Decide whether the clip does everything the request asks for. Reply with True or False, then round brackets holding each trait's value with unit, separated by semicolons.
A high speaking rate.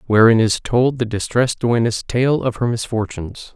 False (170 wpm)